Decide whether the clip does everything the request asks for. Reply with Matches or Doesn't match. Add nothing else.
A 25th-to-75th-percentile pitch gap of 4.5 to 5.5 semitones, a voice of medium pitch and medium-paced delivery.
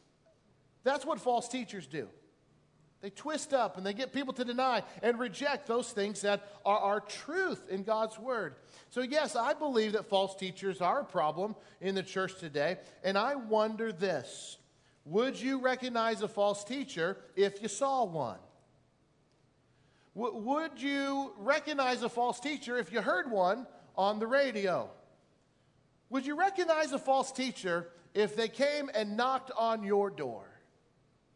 Doesn't match